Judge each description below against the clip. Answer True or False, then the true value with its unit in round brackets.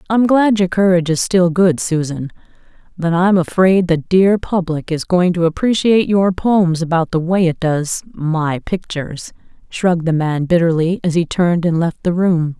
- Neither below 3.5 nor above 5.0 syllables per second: True (4.7 syllables/s)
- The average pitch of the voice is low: False (175 Hz)